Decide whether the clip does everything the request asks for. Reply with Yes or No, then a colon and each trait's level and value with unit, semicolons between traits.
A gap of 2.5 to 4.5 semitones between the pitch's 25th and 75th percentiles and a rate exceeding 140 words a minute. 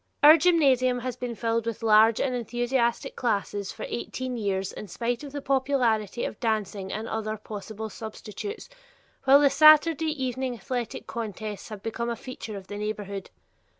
Yes: average, 3.5 semitones; average, 160 wpm